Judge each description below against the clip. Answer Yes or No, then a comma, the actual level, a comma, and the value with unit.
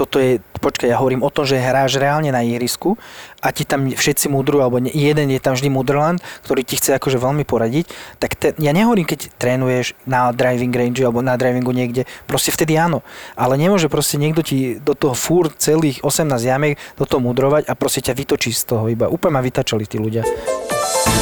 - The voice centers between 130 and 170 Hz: Yes, low, 135 Hz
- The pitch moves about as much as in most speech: Yes, average, 3.1 semitones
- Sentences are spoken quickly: Yes, fast, 200 wpm